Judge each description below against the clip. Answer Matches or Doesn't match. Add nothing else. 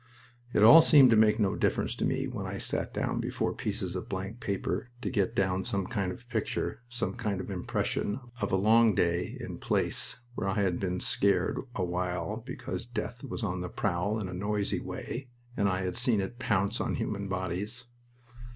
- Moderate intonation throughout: Matches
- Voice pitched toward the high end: Doesn't match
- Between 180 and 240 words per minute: Matches